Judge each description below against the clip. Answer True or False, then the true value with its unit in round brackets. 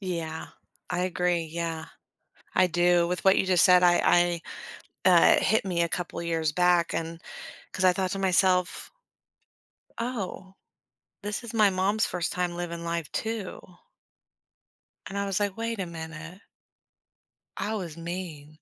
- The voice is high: False (180 Hz)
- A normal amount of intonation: False (2.2 semitones)